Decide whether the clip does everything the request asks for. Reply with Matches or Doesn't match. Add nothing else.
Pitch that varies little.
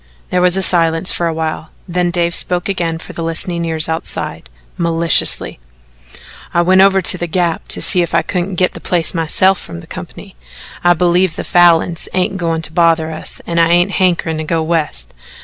Matches